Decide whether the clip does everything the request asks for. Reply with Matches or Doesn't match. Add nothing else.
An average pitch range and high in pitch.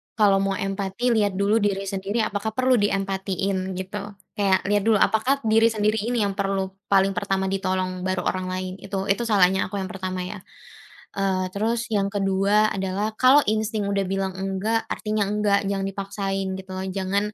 Doesn't match